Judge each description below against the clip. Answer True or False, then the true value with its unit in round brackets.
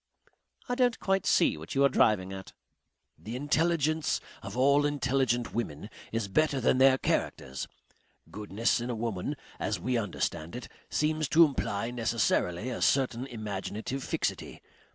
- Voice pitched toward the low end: True (120 Hz)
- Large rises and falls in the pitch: False (5.0 semitones)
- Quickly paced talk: False (145 wpm)